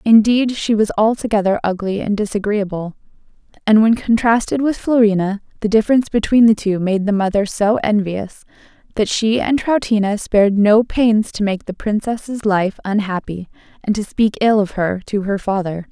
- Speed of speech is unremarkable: Yes, average, 165 wpm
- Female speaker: Yes, female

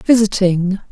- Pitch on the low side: No, high, 195 Hz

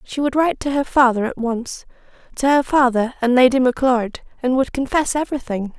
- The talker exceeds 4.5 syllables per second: Yes, 5.5 syllables/s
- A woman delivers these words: Yes, female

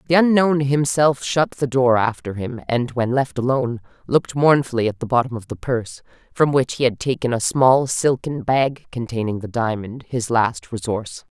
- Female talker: Yes, female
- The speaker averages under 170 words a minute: No, average, 185 wpm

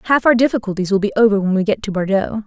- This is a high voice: Yes, high, 210 Hz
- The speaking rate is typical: No, fast, 265 wpm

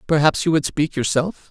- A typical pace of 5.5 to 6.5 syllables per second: No, 5.2 syllables/s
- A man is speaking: Yes, male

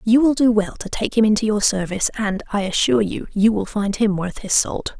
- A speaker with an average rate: No, fast, 250 wpm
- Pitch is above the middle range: Yes, high, 210 Hz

